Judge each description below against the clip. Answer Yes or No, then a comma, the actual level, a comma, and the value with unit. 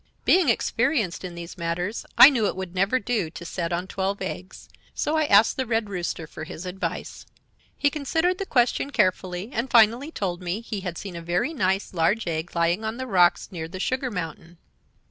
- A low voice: No, high, 195 Hz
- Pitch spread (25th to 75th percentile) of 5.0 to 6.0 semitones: Yes, wide, 5.6 semitones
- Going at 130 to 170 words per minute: No, average, 200 wpm